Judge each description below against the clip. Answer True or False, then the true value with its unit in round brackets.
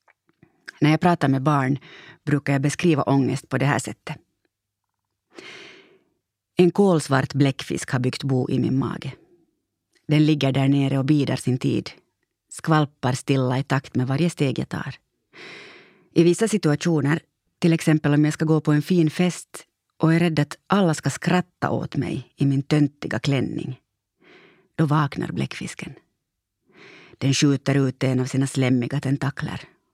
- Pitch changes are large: False (3.8 semitones)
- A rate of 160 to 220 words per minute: False (150 wpm)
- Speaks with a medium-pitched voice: True (145 Hz)